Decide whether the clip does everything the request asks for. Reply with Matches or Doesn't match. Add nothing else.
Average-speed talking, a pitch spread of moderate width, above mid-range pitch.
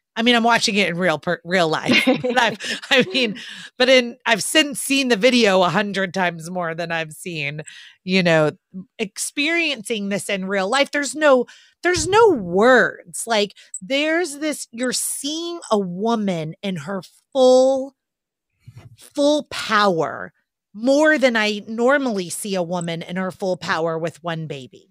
Doesn't match